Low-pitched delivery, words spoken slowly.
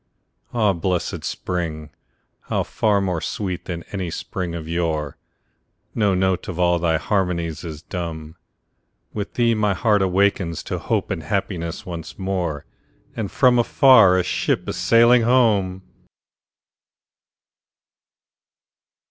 Yes: very low, 90 Hz; slow, 120 wpm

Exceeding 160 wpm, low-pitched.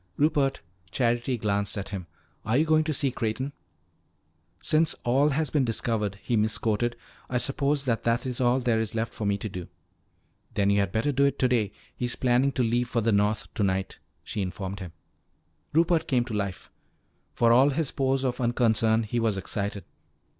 Yes: average, 180 wpm; low, 120 Hz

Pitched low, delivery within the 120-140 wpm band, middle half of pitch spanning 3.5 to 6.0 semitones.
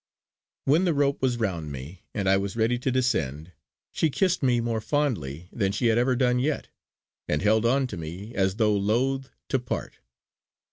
No: low, 115 Hz; average, 185 wpm; average, 5.3 semitones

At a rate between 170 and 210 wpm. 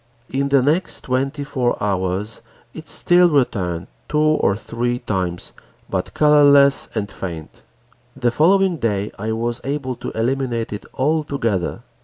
No: slow, 135 wpm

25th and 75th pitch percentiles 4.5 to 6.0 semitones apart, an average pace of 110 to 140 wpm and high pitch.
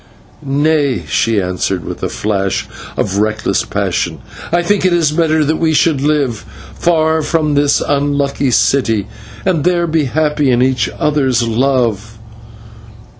No: average, 5.3 semitones; slow, 135 wpm; medium, 140 Hz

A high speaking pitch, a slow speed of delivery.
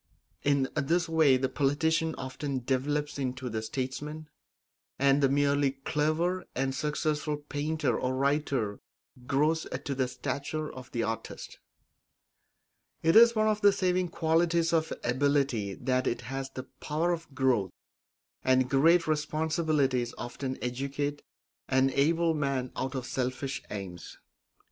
No: medium, 140 Hz; slow, 130 wpm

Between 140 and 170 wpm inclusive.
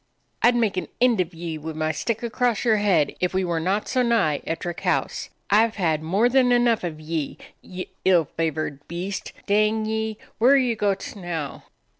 No: average, 200 wpm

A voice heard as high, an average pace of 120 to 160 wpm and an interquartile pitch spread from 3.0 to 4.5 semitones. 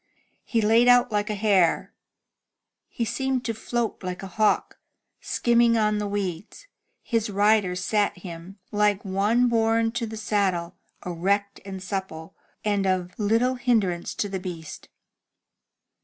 Yes: high, 205 Hz; average, 140 wpm; average, 3.3 semitones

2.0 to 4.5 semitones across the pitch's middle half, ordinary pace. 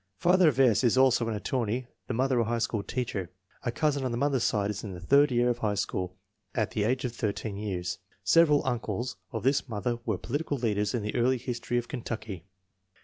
No: average, 3.7 semitones; fast, 215 wpm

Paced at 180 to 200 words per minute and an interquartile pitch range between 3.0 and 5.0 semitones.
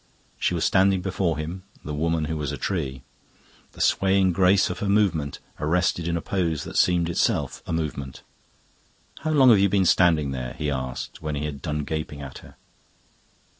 Yes: average, 185 wpm; average, 4.2 semitones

